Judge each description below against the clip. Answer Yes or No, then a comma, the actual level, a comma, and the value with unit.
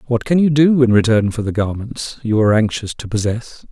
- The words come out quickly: Yes, fast, 225 wpm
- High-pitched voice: No, low, 115 Hz